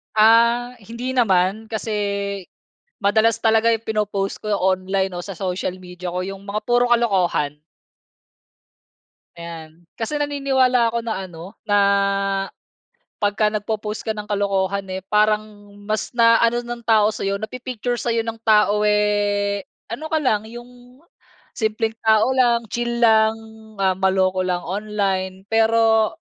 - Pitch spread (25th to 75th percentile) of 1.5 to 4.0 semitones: Yes, average, 2.9 semitones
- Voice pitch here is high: Yes, high, 215 Hz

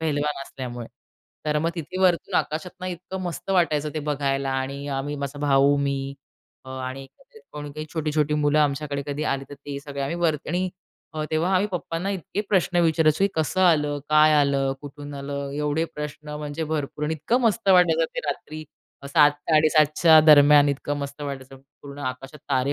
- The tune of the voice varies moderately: No, narrow, 2.3 semitones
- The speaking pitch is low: No, medium, 150 Hz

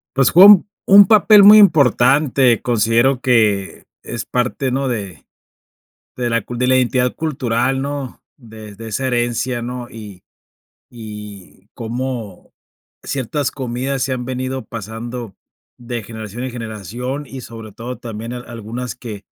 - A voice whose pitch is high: No, low, 120 Hz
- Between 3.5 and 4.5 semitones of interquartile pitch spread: No, average, 2.7 semitones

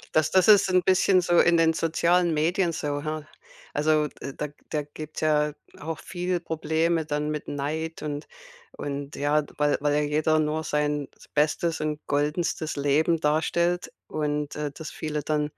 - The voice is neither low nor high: Yes, medium, 155 Hz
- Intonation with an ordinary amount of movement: No, narrow, 1.8 semitones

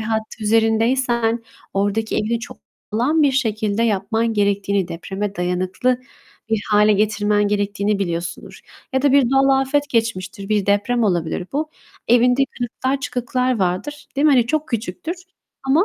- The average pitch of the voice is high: Yes, high, 225 Hz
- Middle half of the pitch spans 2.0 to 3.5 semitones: No, average, 4.0 semitones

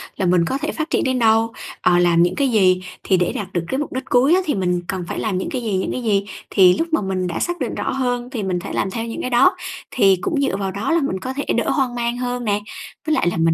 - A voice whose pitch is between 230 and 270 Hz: No, high, 220 Hz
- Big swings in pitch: Yes, wide, 5.8 semitones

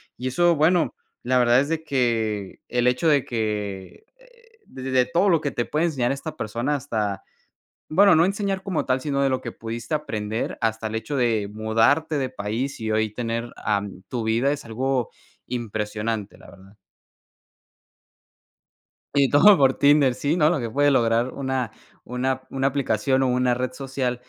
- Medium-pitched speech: No, low, 130 Hz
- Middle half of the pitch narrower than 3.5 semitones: No, average, 4.3 semitones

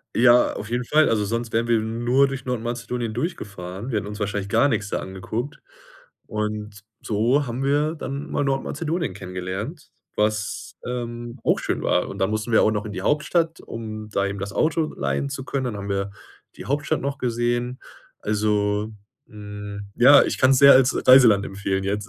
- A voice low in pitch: Yes, low, 115 Hz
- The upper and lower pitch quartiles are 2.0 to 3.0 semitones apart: No, average, 4.3 semitones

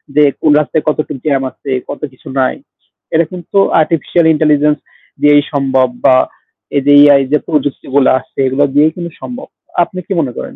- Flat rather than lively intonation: Yes, narrow, 2.3 semitones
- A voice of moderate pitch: Yes, medium, 150 Hz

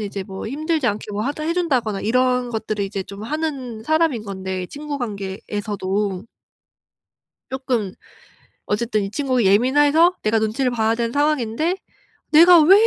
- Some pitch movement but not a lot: No, wide, 5.9 semitones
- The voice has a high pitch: Yes, high, 235 Hz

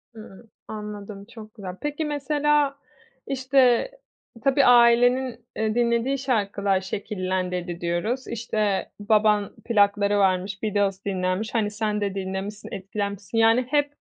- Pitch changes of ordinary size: Yes, average, 3.7 semitones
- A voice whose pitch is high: Yes, high, 210 Hz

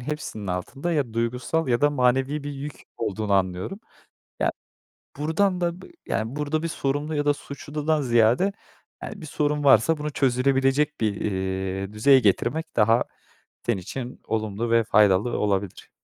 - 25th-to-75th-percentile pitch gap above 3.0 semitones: Yes, wide, 5.4 semitones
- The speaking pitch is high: No, low, 130 Hz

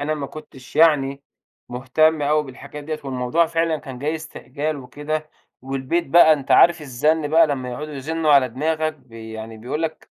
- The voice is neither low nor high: Yes, medium, 150 Hz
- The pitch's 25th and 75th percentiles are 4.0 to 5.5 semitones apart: No, average, 3.1 semitones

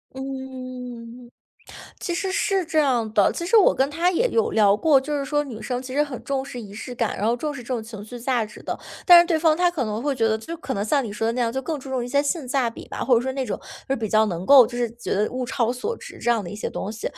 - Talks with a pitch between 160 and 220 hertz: No, very high, 255 Hz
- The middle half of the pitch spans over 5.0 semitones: No, average, 4.0 semitones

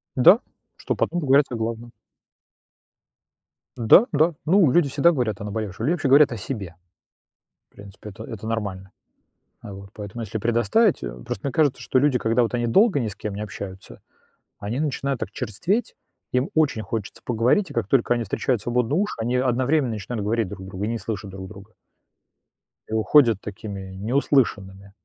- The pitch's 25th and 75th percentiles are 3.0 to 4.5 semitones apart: No, average, 5.1 semitones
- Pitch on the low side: Yes, low, 115 Hz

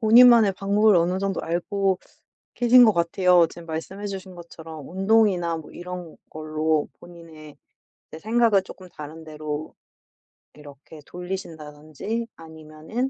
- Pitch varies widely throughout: No, average, 4.0 semitones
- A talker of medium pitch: Yes, medium, 175 Hz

